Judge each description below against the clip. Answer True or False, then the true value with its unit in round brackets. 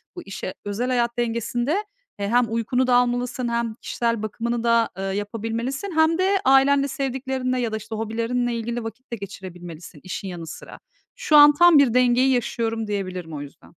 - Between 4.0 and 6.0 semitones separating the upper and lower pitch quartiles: False (3.0 semitones)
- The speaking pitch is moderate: False (235 Hz)